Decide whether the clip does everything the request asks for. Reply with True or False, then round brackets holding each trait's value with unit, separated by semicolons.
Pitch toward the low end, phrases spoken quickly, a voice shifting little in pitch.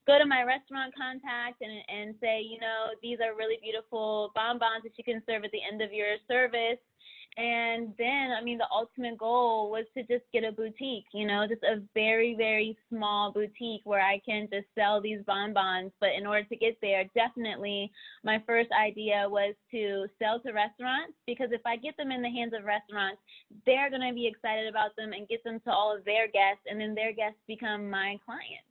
False (220 Hz; 210 wpm; 2.1 semitones)